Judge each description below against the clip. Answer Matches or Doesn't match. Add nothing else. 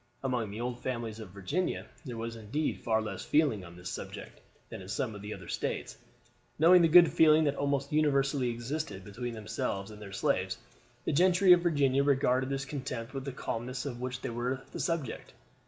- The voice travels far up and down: Doesn't match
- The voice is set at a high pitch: Doesn't match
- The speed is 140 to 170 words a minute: Doesn't match